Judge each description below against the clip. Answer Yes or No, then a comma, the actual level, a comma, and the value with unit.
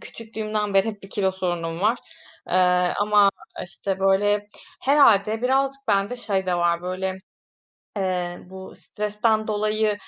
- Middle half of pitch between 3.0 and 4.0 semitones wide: No, narrow, 2.5 semitones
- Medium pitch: No, high, 200 Hz